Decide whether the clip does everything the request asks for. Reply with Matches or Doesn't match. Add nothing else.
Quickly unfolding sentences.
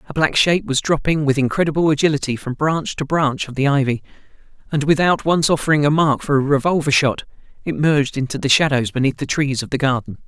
Matches